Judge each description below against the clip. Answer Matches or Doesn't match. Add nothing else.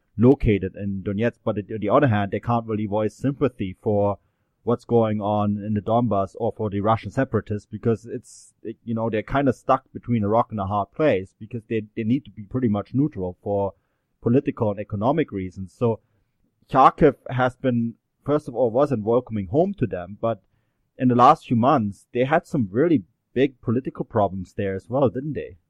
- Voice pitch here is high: Doesn't match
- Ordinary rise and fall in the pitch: Matches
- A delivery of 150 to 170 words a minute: Doesn't match